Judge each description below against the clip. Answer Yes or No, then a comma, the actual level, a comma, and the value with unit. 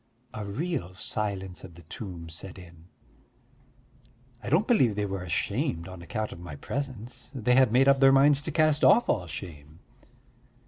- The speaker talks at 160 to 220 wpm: Yes, average, 170 wpm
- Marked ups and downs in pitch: Yes, wide, 7.5 semitones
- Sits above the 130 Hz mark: No, low, 100 Hz